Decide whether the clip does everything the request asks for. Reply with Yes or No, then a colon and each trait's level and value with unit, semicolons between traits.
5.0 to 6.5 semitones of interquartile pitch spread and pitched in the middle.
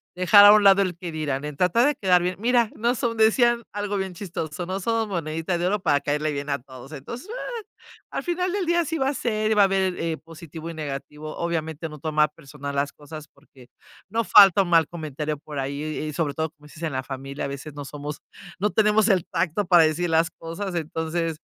Yes: average, 5.3 semitones; medium, 165 Hz